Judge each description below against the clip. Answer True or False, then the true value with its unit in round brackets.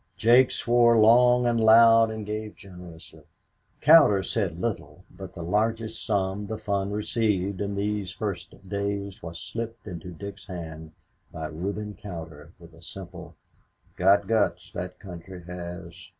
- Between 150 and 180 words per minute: False (140 wpm)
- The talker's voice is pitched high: False (100 Hz)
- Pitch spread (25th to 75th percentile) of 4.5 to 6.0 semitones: False (3.6 semitones)